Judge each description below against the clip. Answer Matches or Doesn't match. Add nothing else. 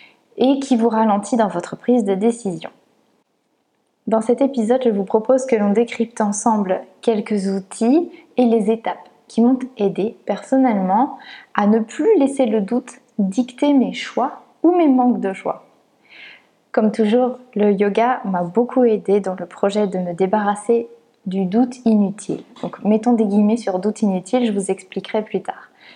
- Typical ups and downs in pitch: Matches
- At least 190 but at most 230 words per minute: Doesn't match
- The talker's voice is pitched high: Matches